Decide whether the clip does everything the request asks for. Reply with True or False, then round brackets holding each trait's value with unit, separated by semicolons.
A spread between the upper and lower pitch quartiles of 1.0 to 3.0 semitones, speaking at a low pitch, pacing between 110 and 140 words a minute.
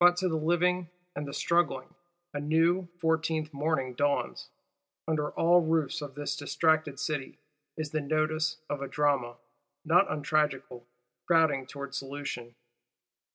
False (2.4 semitones; 155 Hz; 135 wpm)